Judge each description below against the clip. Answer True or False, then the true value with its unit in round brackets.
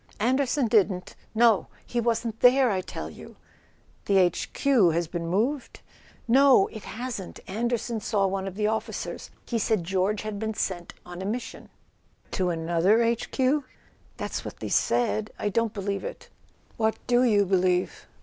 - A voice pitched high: True (215 Hz)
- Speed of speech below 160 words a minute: False (165 wpm)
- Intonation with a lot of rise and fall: False (4.0 semitones)